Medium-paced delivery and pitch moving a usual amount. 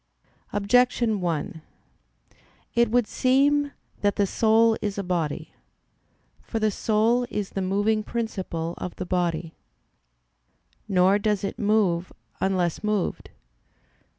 No: slow, 115 wpm; average, 3.6 semitones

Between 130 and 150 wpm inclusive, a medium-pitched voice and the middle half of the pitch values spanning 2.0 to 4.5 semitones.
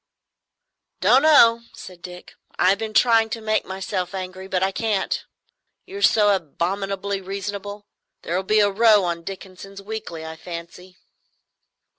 No: average, 140 wpm; high, 195 Hz; average, 2.9 semitones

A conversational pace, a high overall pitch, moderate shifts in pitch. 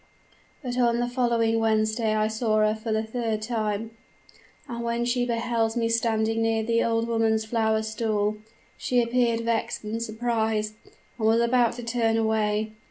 No: average, 165 wpm; high, 225 Hz; narrow, 1.2 semitones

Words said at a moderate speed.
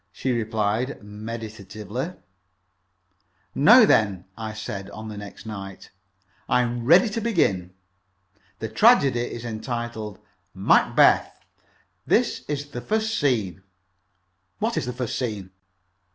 No: slow, 115 wpm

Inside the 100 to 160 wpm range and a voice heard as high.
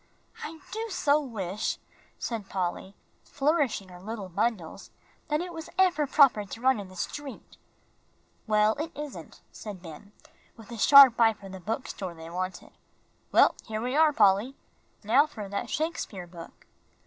Yes: average, 155 wpm; high, 220 Hz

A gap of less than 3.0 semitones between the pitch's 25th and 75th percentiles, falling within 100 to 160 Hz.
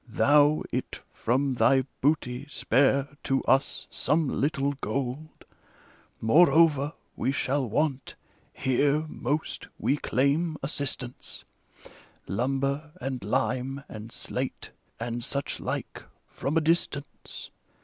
Yes: narrow, 2.4 semitones; medium, 140 Hz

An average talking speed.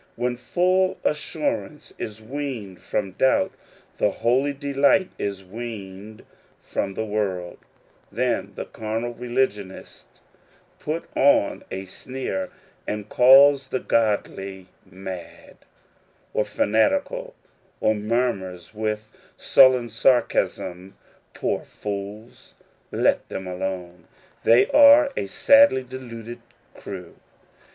No: slow, 105 wpm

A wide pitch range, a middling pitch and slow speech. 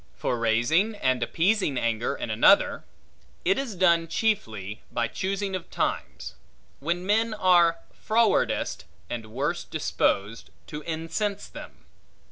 Yes: wide, 8.8 semitones; medium, 165 Hz; slow, 120 wpm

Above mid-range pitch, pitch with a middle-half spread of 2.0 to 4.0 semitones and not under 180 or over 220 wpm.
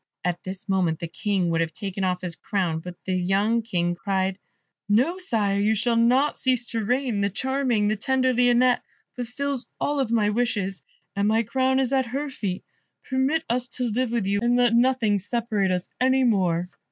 No: high, 225 Hz; average, 4.6 semitones; average, 190 wpm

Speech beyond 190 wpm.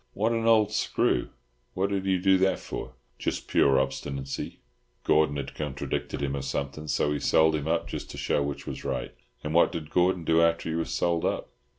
Yes: average, 200 wpm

